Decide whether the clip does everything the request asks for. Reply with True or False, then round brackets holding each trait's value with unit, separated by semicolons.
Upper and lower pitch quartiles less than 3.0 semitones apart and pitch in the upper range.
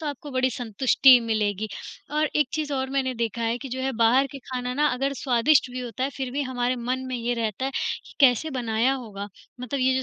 True (2.4 semitones; 255 Hz)